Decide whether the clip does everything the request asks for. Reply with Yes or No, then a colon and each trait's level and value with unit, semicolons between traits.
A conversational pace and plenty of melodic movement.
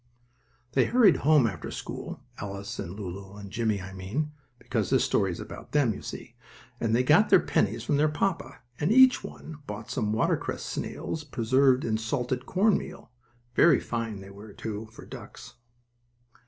Yes: average, 170 wpm; wide, 6.4 semitones